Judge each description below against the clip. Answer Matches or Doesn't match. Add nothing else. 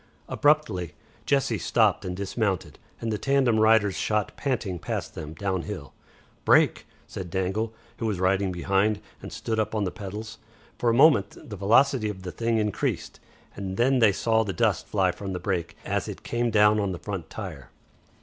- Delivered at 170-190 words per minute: Matches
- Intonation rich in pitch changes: Doesn't match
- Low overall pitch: Matches